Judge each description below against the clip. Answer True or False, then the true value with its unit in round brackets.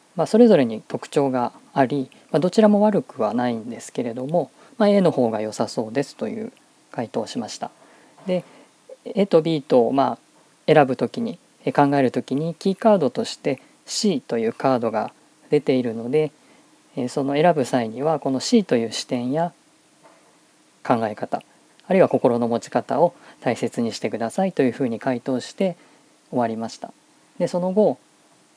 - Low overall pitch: False (155 Hz)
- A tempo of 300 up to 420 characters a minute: True (315 characters per minute)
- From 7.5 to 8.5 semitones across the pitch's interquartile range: True (8.0 semitones)